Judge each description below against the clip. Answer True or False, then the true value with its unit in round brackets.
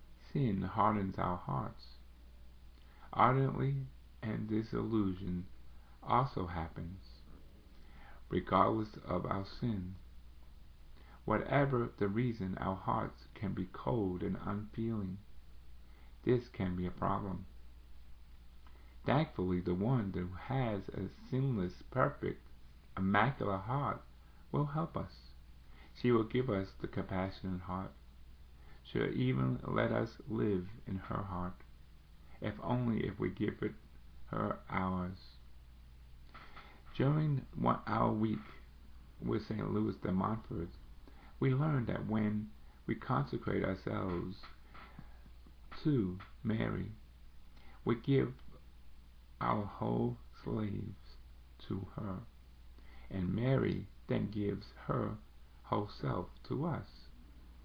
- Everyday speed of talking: False (100 wpm)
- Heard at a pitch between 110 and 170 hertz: False (90 Hz)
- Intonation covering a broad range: True (8.7 semitones)